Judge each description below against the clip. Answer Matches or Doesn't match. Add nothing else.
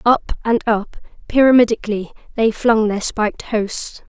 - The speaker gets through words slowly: Matches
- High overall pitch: Matches